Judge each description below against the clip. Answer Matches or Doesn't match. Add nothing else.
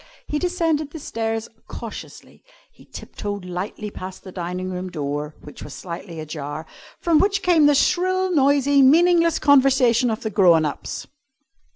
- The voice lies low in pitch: Doesn't match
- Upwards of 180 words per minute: Doesn't match